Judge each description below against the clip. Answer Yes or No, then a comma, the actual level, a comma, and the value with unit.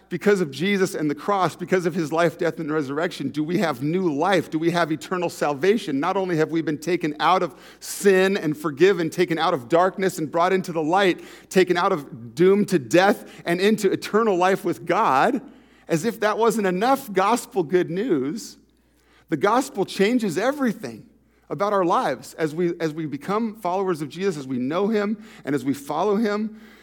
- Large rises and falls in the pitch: No, average, 3.5 semitones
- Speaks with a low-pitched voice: No, medium, 185 Hz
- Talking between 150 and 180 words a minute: No, average, 195 wpm